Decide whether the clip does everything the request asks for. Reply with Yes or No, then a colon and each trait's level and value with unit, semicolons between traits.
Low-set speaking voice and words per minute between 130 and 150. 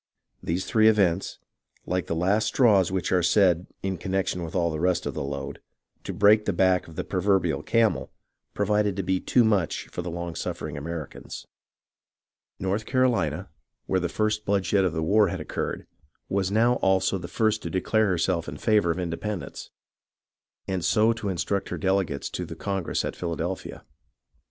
No: very low, 95 Hz; average, 175 wpm